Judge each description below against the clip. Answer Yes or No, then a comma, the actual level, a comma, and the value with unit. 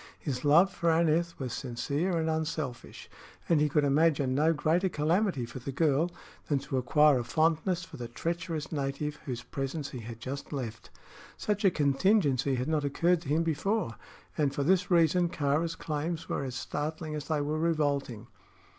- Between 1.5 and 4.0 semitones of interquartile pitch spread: Yes, average, 3.3 semitones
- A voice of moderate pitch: Yes, medium, 150 Hz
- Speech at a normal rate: Yes, average, 175 wpm